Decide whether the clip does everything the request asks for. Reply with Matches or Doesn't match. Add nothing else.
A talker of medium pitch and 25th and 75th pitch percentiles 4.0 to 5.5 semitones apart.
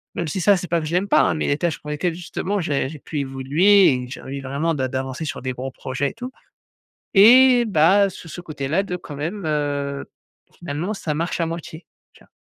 Matches